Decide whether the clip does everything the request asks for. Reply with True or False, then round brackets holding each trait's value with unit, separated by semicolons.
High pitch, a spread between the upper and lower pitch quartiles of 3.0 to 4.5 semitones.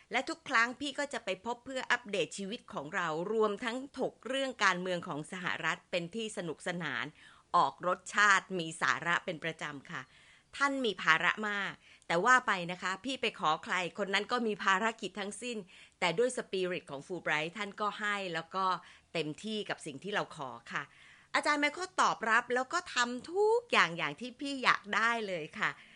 False (205 Hz; 5.2 semitones)